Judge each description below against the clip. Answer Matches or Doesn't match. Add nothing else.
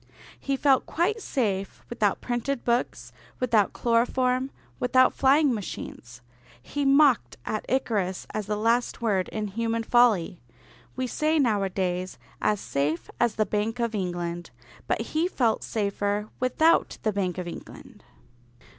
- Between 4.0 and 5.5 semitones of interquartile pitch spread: Matches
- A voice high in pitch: Matches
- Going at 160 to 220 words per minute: Doesn't match